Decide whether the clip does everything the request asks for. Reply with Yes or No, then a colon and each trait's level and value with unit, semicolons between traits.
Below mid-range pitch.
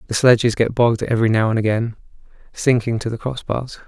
Yes: low, 115 Hz